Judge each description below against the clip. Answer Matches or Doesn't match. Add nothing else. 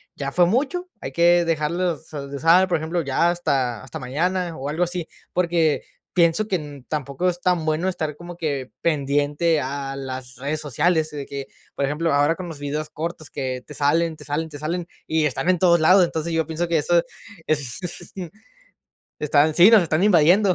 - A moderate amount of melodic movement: Matches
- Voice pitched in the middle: Matches